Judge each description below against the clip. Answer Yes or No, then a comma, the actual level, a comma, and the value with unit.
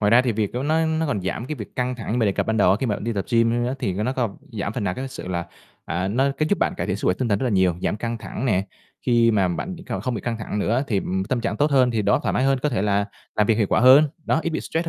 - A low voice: Yes, low, 115 Hz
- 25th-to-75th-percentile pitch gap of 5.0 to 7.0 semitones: No, average, 4.1 semitones